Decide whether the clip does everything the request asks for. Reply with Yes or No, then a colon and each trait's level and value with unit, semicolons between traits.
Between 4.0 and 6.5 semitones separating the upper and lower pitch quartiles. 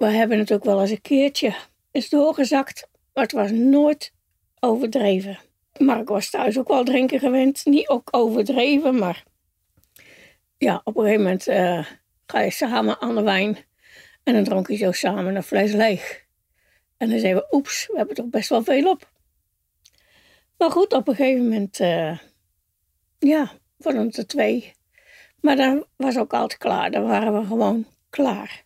Yes: wide, 5.6 semitones